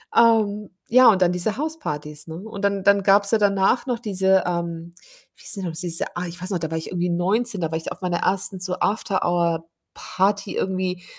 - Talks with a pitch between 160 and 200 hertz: Yes, high, 190 Hz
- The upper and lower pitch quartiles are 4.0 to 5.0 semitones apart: No, average, 2.8 semitones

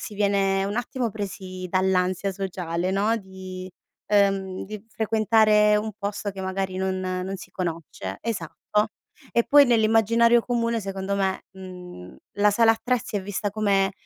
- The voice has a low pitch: No, high, 195 Hz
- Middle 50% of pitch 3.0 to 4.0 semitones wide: No, narrow, 2.5 semitones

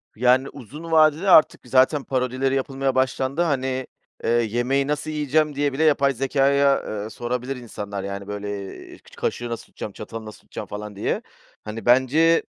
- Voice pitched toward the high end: No, low, 130 Hz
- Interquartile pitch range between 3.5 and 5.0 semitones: Yes, average, 3.8 semitones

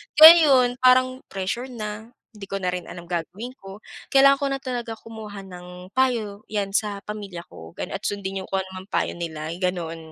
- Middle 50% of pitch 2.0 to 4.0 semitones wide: No, average, 4.9 semitones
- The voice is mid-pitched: No, high, 205 Hz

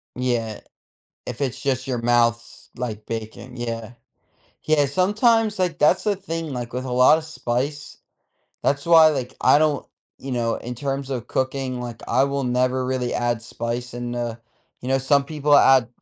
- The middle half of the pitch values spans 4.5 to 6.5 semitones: No, average, 3.0 semitones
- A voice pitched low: Yes, low, 130 Hz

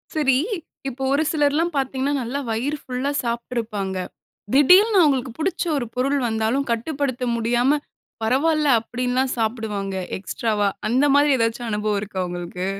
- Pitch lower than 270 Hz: Yes, very high, 250 Hz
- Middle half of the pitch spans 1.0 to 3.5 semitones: No, average, 4.2 semitones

